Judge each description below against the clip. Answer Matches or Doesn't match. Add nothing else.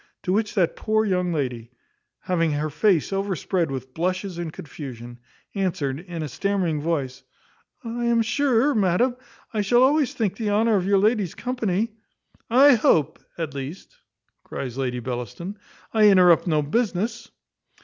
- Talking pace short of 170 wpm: Matches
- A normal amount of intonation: Doesn't match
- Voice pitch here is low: Doesn't match